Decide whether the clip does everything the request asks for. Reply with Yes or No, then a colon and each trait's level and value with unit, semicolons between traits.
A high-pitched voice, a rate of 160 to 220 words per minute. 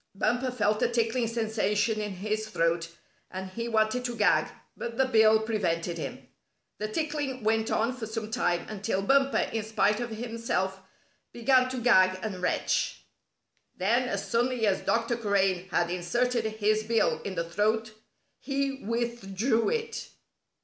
No: high, 220 Hz; average, 150 wpm